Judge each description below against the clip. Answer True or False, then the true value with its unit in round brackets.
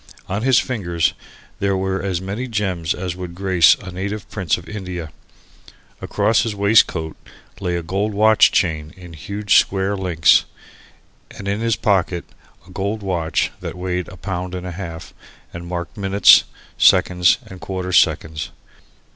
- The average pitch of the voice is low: True (95 Hz)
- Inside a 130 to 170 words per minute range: True (155 wpm)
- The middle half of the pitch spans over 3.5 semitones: False (2.5 semitones)